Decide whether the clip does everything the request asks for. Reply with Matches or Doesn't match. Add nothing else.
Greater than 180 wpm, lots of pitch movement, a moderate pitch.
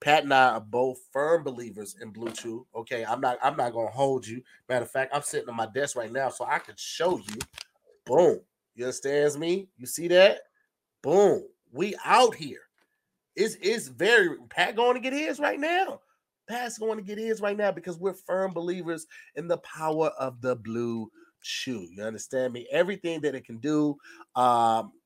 Matches